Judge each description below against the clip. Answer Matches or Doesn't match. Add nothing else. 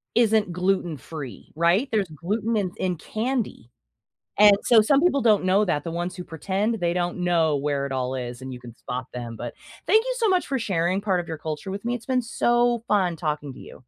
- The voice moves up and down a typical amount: Doesn't match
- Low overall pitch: Doesn't match